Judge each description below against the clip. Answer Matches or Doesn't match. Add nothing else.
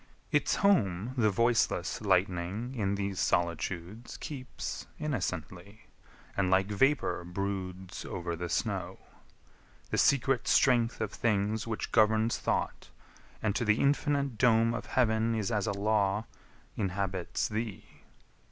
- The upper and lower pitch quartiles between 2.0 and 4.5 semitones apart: Matches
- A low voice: Matches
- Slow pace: Matches